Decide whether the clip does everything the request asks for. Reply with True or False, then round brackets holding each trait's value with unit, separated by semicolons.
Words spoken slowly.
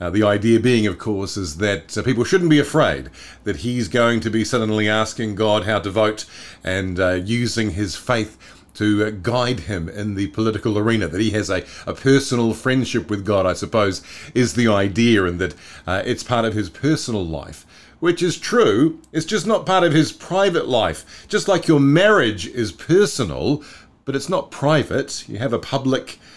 False (195 wpm)